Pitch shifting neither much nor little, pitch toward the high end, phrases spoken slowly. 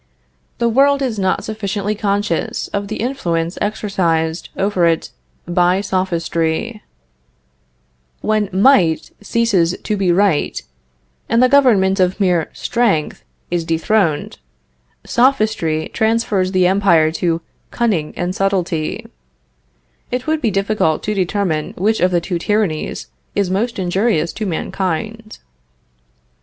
Yes: average, 4.1 semitones; high, 195 Hz; slow, 120 wpm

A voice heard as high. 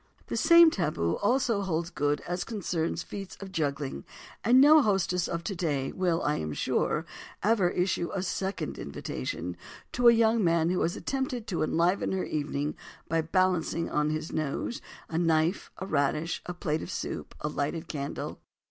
No: medium, 170 Hz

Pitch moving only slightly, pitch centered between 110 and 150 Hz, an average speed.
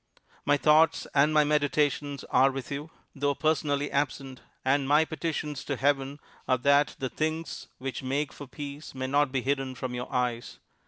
Yes: narrow, 1.8 semitones; medium, 140 Hz; average, 170 wpm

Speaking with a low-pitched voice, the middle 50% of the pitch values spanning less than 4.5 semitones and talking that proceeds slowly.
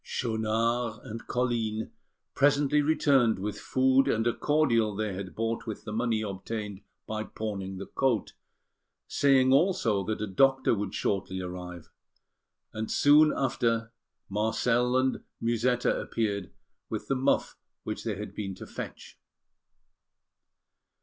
Yes: low, 115 Hz; average, 3.6 semitones; slow, 125 wpm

